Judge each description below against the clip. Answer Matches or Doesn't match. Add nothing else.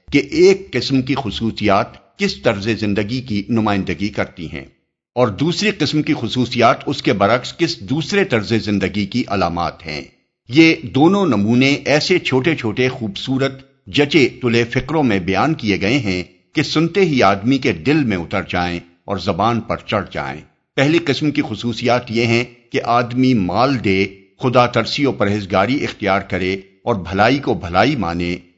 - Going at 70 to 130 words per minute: Doesn't match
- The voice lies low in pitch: Matches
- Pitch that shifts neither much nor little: Doesn't match